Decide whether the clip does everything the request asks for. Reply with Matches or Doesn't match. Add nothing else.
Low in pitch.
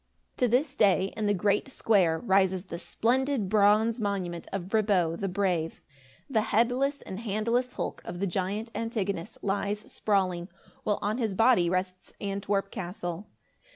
Doesn't match